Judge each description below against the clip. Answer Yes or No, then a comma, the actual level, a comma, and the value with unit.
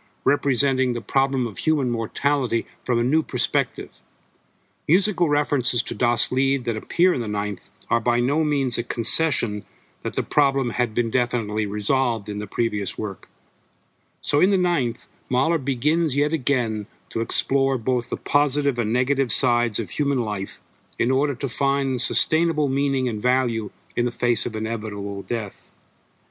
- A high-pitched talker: No, low, 125 Hz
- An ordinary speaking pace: Yes, average, 160 wpm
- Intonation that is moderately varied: Yes, average, 3.4 semitones